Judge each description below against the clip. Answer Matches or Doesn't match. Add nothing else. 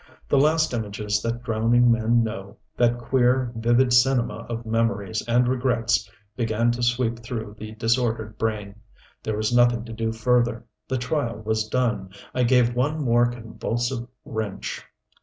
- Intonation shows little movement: Matches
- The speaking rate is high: Doesn't match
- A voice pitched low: Matches